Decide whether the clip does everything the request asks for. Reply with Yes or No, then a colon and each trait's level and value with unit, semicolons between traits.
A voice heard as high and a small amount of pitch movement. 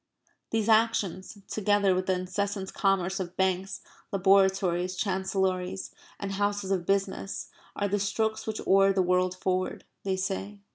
Yes: high, 195 Hz; narrow, 1.5 semitones